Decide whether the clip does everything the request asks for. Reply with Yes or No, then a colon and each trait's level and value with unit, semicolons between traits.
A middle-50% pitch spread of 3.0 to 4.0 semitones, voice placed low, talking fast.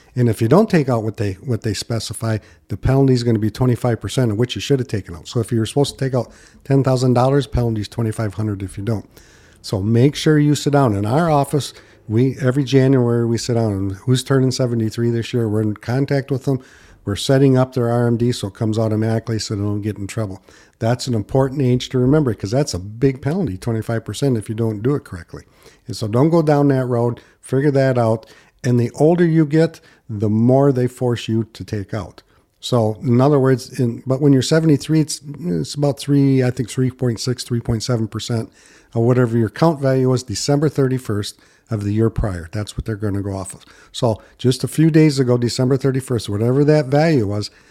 Yes: average, 3.5 semitones; low, 120 Hz; fast, 225 wpm